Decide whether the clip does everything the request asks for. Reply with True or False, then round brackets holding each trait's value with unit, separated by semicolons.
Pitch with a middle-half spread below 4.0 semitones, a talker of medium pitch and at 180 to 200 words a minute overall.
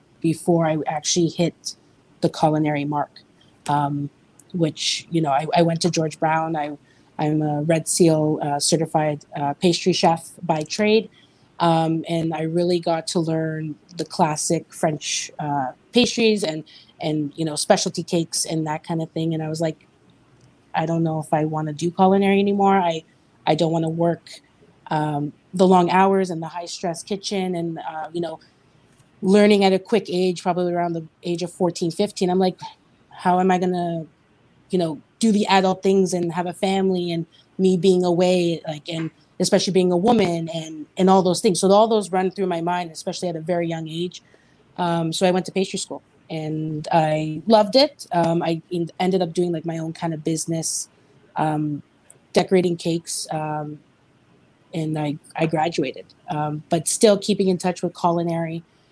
True (2.7 semitones; 170 Hz; 185 wpm)